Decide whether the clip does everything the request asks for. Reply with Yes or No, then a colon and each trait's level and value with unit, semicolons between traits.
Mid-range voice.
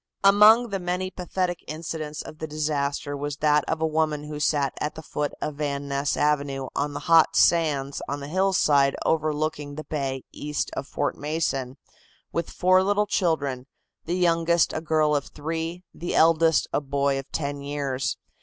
Yes: medium, 150 Hz